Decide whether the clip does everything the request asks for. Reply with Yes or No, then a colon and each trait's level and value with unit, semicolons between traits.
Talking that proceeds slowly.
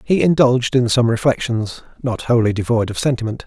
No: average, 155 wpm